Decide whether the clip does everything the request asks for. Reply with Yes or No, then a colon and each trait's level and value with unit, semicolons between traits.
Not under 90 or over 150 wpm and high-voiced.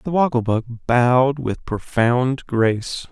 No: slow, 135 wpm; low, 125 Hz